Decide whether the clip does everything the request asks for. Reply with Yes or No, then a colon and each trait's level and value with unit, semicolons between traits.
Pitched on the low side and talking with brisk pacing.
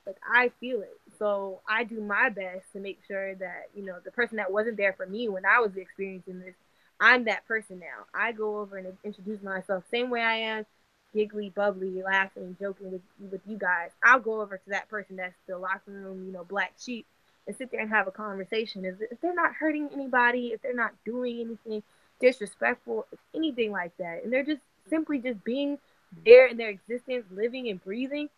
No: high, 215 Hz; fast, 215 wpm